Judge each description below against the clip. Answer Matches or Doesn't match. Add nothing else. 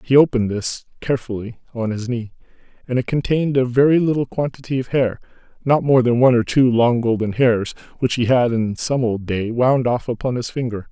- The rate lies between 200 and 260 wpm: Matches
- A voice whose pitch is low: Matches